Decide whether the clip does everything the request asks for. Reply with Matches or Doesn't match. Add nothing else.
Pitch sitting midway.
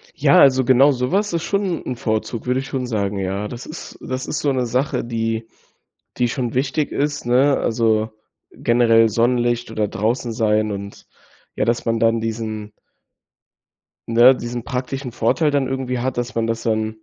Doesn't match